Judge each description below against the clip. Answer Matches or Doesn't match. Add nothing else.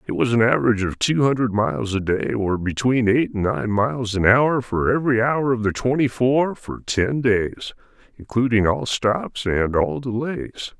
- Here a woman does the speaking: Doesn't match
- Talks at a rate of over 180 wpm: Matches